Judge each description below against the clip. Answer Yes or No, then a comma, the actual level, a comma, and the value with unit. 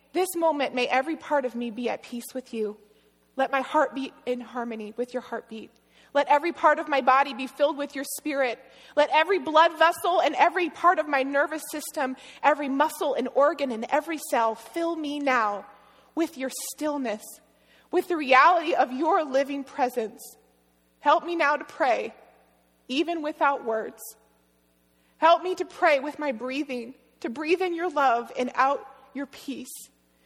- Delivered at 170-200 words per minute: Yes, average, 175 wpm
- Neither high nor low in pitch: No, very high, 275 Hz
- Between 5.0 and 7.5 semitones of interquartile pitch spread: No, average, 3.8 semitones